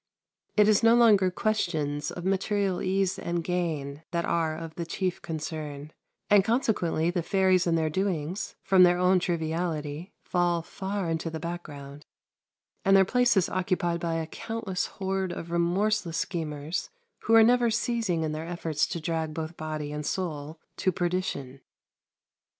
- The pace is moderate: Yes, average, 155 wpm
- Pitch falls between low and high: Yes, medium, 175 Hz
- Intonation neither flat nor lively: Yes, average, 3.3 semitones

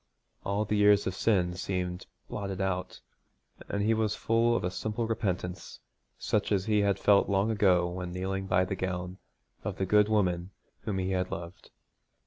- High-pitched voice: No, very low, 95 Hz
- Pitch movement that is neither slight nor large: No, narrow, 2.3 semitones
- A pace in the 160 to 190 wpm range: Yes, average, 175 wpm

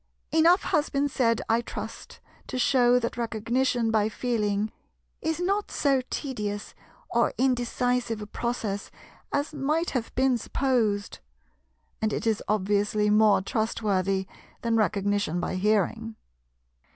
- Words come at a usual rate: No, slow, 125 wpm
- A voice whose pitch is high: Yes, high, 230 Hz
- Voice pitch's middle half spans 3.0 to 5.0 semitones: Yes, average, 3.7 semitones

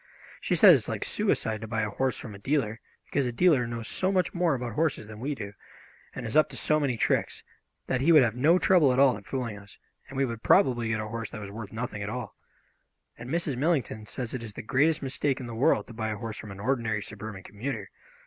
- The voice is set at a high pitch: No, low, 120 Hz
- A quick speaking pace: Yes, fast, 255 wpm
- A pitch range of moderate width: Yes, average, 4.1 semitones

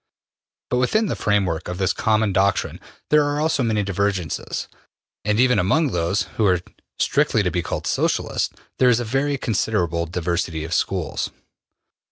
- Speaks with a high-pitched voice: No, low, 100 Hz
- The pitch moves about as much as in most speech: No, wide, 5.7 semitones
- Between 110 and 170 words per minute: Yes, average, 155 wpm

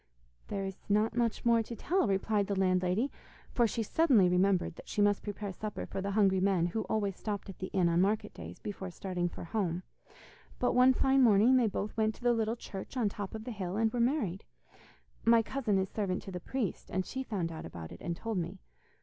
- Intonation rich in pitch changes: No, average, 3.4 semitones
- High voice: Yes, high, 205 Hz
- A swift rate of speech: Yes, fast, 225 wpm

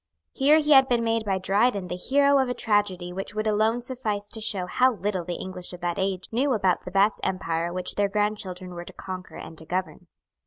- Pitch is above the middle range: Yes, high, 200 Hz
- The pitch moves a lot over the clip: No, average, 3.9 semitones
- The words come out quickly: Yes, fast, 225 wpm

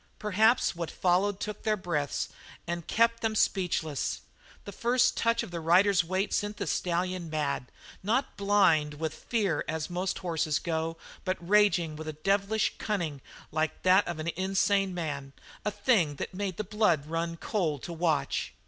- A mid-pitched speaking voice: Yes, medium, 180 Hz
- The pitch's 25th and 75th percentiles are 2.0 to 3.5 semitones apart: No, average, 4.2 semitones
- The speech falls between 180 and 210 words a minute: No, average, 165 wpm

